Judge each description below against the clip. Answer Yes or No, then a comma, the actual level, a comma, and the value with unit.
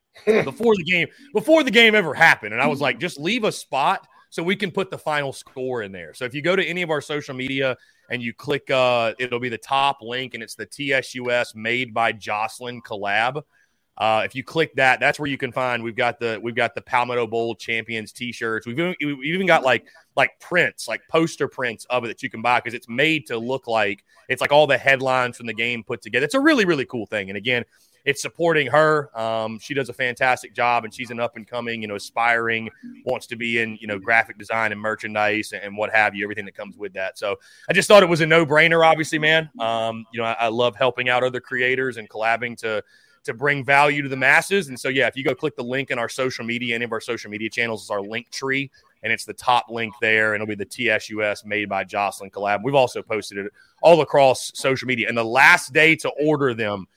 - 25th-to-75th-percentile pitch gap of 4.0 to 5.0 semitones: Yes, average, 4.3 semitones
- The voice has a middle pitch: No, low, 125 Hz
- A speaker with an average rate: No, fast, 240 wpm